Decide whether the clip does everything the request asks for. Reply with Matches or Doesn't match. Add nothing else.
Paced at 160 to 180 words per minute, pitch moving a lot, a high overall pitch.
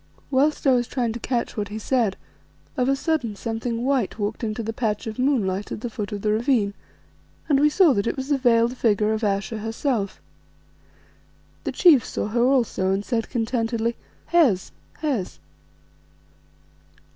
Doesn't match